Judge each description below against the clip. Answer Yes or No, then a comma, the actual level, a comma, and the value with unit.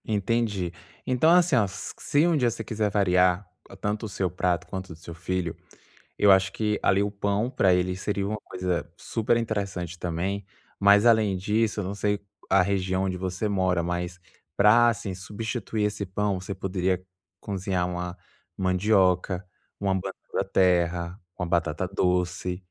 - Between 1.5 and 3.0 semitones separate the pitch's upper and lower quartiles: Yes, narrow, 2.5 semitones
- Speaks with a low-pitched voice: Yes, very low, 95 Hz